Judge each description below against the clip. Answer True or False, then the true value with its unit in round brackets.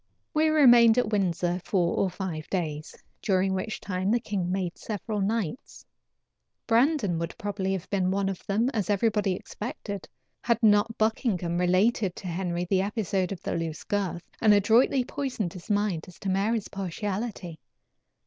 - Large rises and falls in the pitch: False (3.4 semitones)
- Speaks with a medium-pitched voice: False (195 Hz)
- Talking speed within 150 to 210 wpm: True (160 wpm)